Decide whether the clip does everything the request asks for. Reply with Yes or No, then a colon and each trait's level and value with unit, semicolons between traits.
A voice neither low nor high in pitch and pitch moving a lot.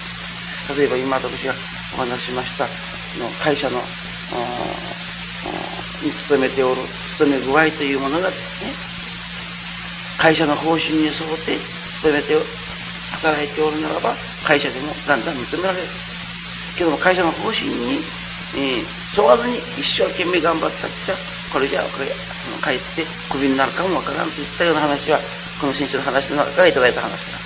No: medium, 160 Hz; average, 3.4 semitones